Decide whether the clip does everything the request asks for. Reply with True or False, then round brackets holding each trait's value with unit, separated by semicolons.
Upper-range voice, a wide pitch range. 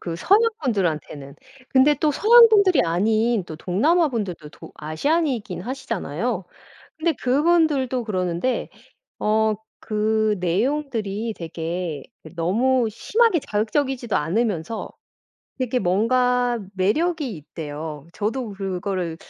True (220 Hz; 6.8 semitones)